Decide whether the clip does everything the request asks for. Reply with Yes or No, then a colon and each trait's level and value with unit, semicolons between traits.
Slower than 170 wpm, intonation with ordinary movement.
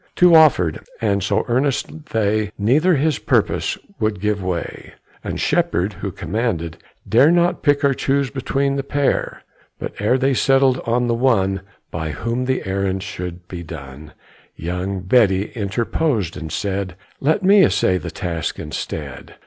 No: average, 150 wpm; wide, 6.6 semitones